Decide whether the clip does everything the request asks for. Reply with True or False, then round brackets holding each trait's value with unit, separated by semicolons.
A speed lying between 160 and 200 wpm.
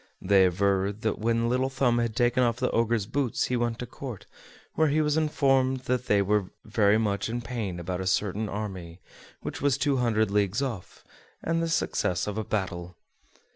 True (190 wpm)